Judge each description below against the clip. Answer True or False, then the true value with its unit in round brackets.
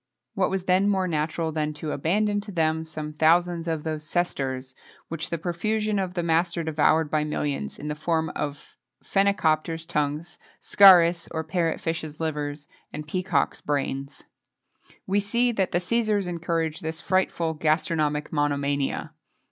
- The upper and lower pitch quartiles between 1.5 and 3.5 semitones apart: True (3.0 semitones)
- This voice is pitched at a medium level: True (160 Hz)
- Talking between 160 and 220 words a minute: False (150 wpm)